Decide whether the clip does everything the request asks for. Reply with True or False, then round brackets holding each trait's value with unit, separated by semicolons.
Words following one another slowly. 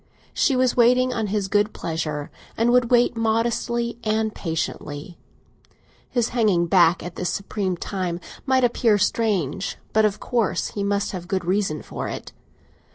False (160 wpm)